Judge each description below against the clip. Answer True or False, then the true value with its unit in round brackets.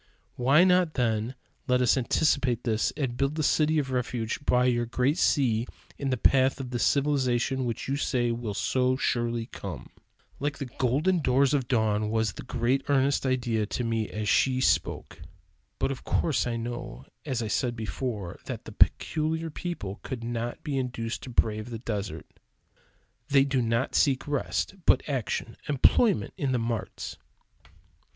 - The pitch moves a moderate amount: True (3.0 semitones)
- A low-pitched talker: True (125 Hz)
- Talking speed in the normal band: True (165 wpm)